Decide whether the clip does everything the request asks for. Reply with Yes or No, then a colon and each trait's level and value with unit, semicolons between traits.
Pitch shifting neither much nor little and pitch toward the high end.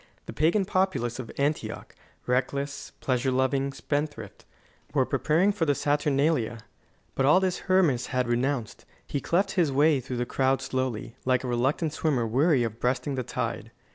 No: average, 3.5 semitones; low, 135 Hz